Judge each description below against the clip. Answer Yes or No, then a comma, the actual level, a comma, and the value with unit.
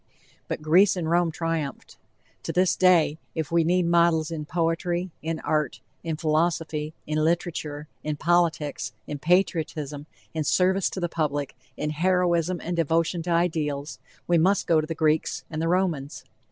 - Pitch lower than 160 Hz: No, medium, 165 Hz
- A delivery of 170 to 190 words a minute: No, average, 160 wpm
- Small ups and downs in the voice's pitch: Yes, narrow, 2.1 semitones